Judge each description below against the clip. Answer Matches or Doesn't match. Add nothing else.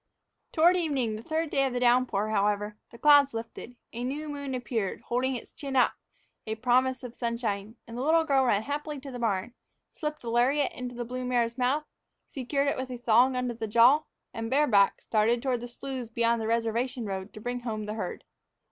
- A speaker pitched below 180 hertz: Doesn't match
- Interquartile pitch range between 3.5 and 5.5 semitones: Doesn't match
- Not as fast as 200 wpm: Doesn't match